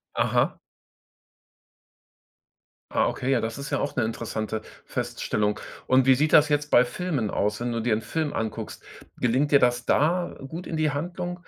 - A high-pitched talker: No, low, 135 Hz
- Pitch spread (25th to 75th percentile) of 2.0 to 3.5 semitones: No, average, 5.0 semitones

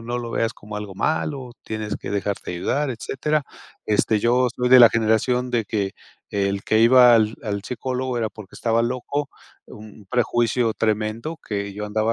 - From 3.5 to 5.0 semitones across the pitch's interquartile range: No, average, 2.9 semitones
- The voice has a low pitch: Yes, low, 115 Hz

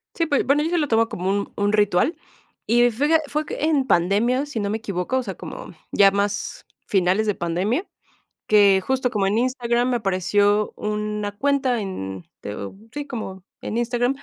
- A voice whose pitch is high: Yes, high, 215 Hz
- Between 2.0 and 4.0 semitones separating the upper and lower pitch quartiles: No, average, 4.5 semitones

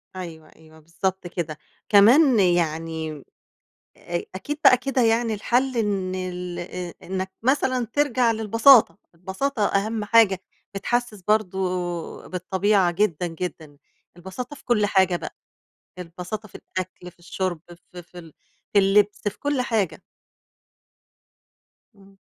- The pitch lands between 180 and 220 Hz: Yes, high, 190 Hz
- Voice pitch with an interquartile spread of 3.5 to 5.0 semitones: Yes, average, 4.3 semitones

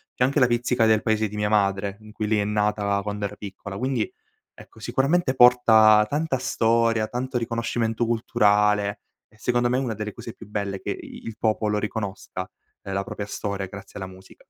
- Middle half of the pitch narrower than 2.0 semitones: No, narrow, 2.6 semitones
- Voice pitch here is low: Yes, low, 110 Hz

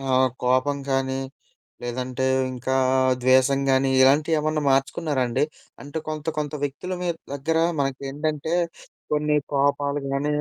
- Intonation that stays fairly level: Yes, narrow, 2.3 semitones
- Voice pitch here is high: No, medium, 140 Hz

